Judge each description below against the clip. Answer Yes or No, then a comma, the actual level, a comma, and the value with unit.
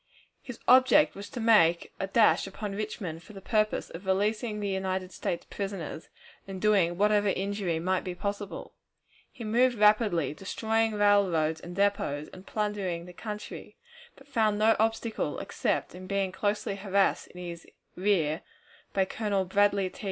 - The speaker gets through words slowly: No, average, 155 wpm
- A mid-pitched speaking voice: No, high, 200 Hz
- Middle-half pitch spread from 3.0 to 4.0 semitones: No, narrow, 2.5 semitones